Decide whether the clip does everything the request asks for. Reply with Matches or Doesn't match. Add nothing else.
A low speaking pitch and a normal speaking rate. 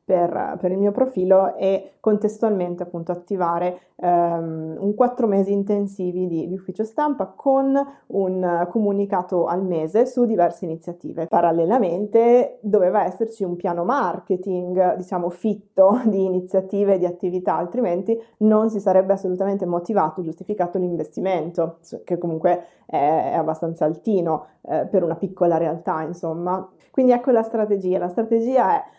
Doesn't match